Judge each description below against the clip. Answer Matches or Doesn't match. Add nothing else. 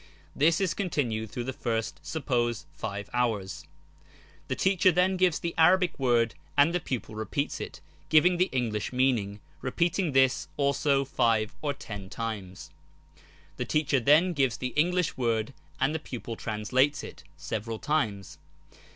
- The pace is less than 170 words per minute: Matches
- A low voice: Matches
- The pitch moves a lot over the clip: Matches